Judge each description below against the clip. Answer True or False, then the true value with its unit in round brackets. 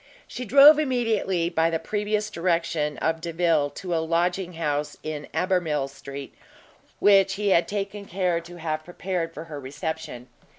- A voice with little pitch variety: False (3.6 semitones)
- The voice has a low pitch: False (170 Hz)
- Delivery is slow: False (155 wpm)